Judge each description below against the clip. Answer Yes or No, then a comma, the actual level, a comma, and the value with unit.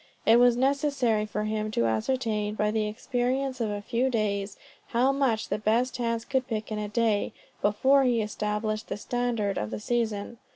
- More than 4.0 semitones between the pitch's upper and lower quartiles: No, average, 2.8 semitones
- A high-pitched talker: Yes, high, 225 Hz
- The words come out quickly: No, average, 180 wpm